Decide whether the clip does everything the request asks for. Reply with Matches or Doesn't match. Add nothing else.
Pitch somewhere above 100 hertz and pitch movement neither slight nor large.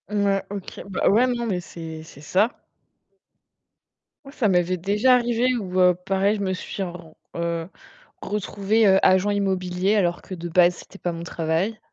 Matches